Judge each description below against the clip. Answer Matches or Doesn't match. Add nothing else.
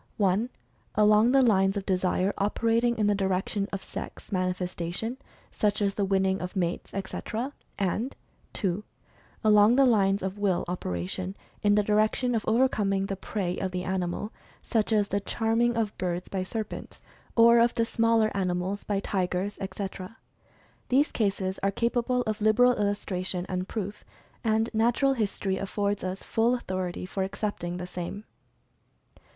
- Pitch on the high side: Matches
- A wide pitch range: Doesn't match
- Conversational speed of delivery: Matches